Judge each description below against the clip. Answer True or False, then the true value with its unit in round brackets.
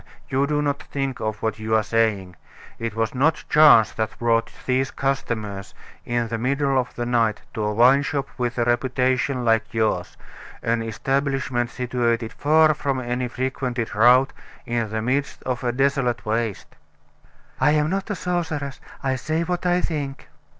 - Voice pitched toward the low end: True (125 Hz)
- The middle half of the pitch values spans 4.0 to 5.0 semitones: False (3.4 semitones)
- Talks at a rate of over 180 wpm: False (165 wpm)